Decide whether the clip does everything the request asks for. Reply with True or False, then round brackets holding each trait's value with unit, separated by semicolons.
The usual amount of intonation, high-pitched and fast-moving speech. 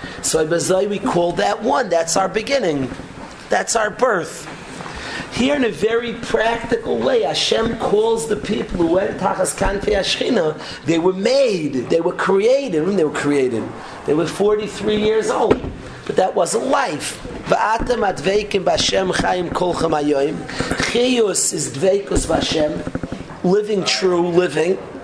False (3.7 semitones; 200 Hz; 150 wpm)